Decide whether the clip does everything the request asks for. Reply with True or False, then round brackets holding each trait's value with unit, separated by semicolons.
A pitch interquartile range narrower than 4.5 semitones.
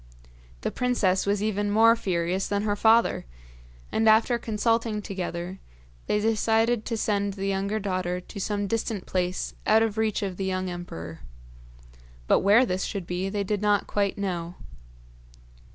True (2.8 semitones)